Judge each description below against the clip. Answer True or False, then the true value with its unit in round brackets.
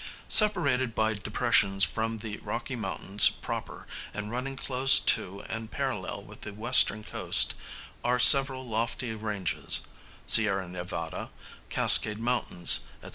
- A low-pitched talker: True (110 Hz)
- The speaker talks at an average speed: False (125 wpm)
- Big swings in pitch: False (3.4 semitones)